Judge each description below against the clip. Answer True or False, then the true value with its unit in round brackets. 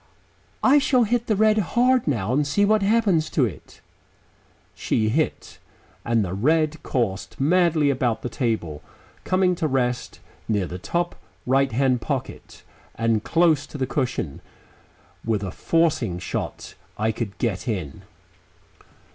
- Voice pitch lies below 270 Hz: True (135 Hz)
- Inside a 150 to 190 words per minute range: False (140 wpm)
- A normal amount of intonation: False (7.7 semitones)